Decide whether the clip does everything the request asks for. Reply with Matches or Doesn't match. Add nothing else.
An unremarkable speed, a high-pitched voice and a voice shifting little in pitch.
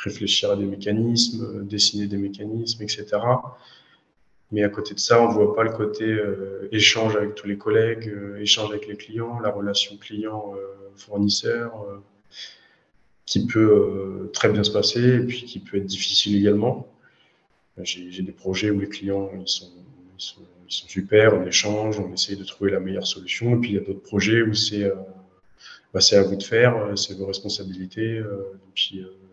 Doesn't match